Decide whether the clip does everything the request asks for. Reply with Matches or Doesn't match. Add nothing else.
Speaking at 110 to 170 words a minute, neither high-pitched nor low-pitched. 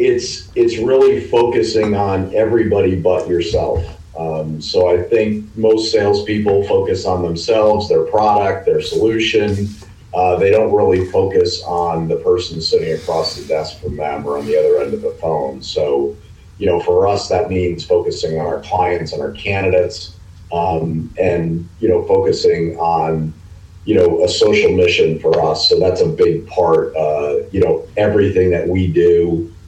Doesn't match